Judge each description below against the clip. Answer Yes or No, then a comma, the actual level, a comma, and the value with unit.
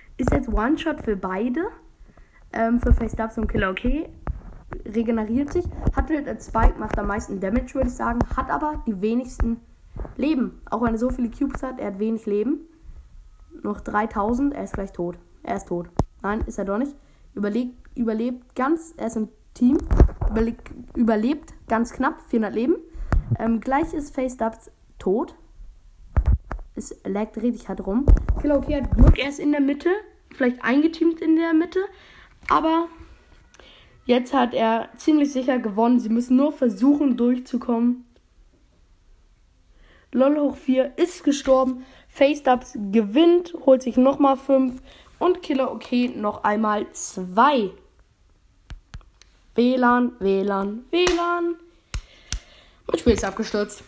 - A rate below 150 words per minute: Yes, average, 140 wpm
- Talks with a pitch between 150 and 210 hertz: No, high, 245 Hz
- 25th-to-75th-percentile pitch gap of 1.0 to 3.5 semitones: No, average, 4.7 semitones